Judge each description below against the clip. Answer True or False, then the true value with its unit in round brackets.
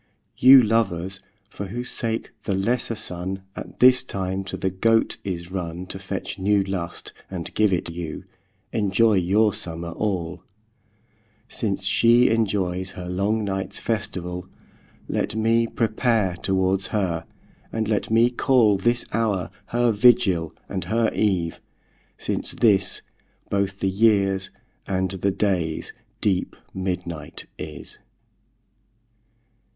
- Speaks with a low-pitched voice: True (95 Hz)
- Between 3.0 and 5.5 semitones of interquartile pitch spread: True (3.3 semitones)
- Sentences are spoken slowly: True (125 wpm)